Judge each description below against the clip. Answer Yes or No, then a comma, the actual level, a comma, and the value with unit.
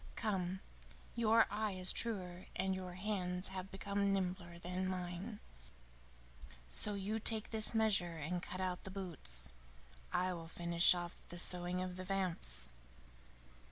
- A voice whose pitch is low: No, medium, 185 Hz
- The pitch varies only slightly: Yes, narrow, 2.1 semitones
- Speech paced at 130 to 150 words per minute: Yes, average, 140 wpm